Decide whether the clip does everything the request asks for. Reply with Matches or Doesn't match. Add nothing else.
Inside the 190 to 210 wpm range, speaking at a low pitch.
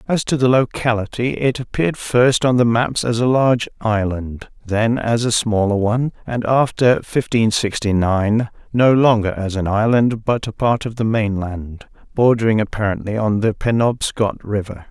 Doesn't match